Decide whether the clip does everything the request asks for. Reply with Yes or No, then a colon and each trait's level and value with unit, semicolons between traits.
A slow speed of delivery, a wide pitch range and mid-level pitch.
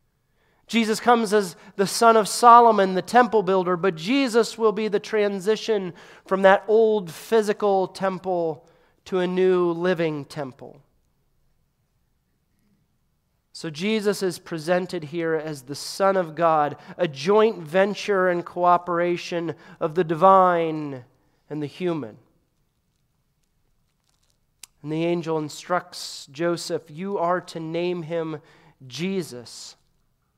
No: slow, 115 wpm; average, 3.5 semitones; medium, 180 Hz